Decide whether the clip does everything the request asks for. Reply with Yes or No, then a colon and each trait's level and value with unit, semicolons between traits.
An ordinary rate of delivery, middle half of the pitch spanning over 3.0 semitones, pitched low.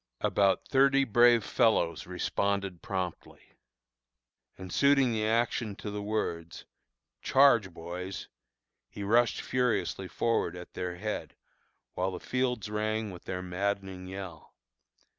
No: slow, 120 wpm; average, 4.1 semitones; low, 100 Hz